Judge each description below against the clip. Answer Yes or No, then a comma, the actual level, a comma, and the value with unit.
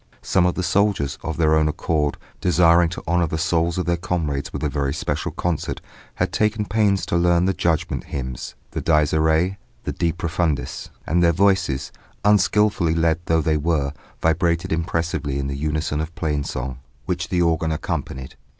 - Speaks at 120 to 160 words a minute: No, average, 175 wpm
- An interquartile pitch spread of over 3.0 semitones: No, narrow, 2.4 semitones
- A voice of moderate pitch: No, very low, 80 Hz